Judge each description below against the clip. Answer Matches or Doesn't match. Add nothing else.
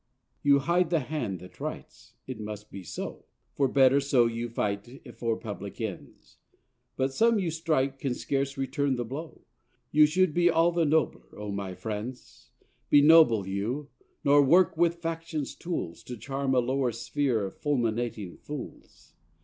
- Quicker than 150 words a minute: Matches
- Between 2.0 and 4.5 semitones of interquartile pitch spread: Doesn't match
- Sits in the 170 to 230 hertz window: Doesn't match